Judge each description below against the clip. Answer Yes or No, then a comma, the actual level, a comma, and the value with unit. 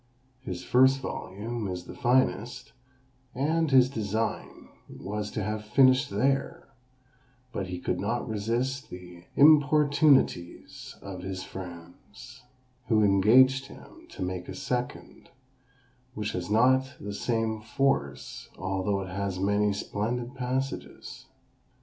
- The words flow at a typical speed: No, slow, 120 wpm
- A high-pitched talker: No, low, 110 Hz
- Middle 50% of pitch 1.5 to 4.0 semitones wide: No, average, 5.3 semitones